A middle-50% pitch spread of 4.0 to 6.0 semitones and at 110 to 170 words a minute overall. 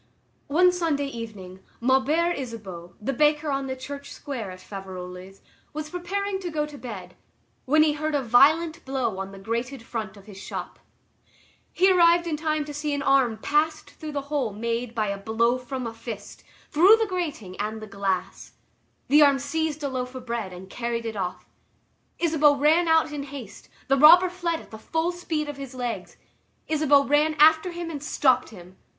No: wide, 5.6 semitones; average, 185 wpm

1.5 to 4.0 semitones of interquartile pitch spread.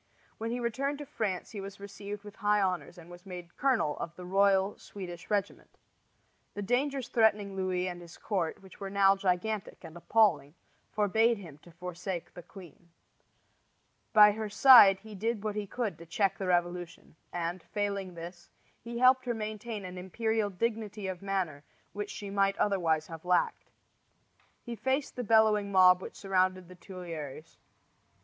Yes: average, 3.1 semitones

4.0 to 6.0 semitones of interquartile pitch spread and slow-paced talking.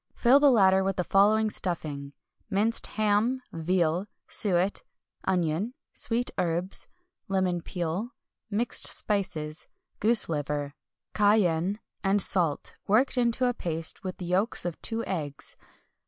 Yes: average, 4.3 semitones; slow, 125 wpm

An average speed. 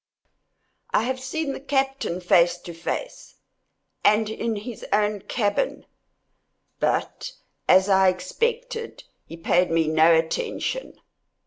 No: slow, 110 wpm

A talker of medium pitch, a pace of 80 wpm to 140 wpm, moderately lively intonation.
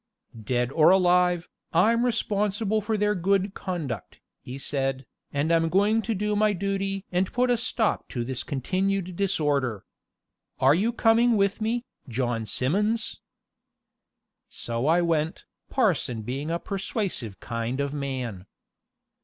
No: medium, 180 Hz; slow, 135 wpm; wide, 7.5 semitones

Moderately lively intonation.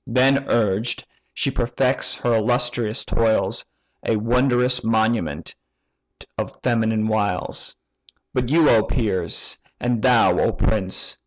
No: narrow, 2.3 semitones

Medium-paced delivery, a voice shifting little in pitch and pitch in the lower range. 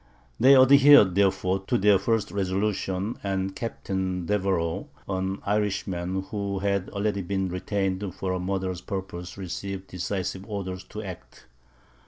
No: slow, 130 wpm; narrow, 1.6 semitones; very low, 95 Hz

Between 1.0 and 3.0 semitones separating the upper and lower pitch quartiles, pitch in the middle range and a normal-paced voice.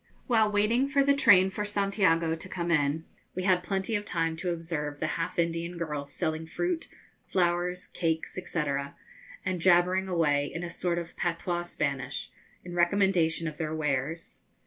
Yes: average, 2.7 semitones; medium, 175 Hz; average, 165 wpm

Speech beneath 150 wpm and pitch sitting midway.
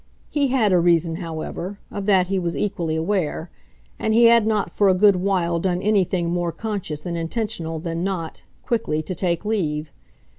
No: average, 180 wpm; medium, 180 Hz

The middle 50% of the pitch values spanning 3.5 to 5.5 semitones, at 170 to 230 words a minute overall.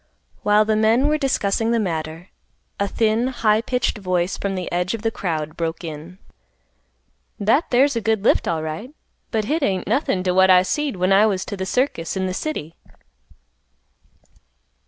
Yes: average, 4.1 semitones; average, 175 wpm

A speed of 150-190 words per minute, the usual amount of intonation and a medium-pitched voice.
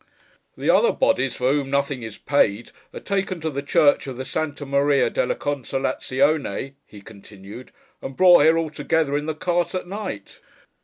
Yes: average, 165 wpm; average, 3.5 semitones; medium, 145 Hz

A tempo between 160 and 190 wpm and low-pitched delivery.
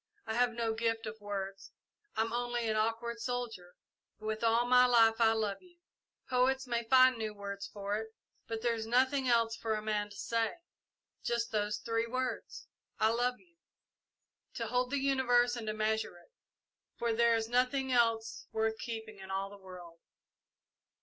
No: average, 175 wpm; high, 230 Hz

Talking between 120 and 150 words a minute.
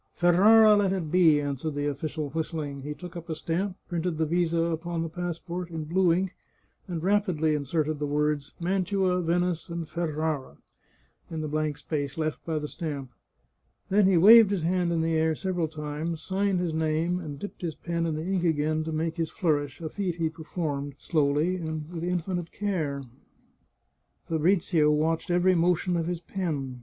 No: average, 185 wpm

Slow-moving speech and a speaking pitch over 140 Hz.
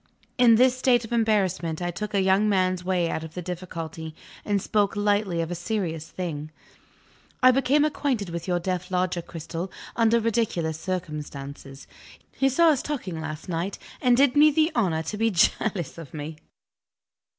No: average, 170 wpm; medium, 185 Hz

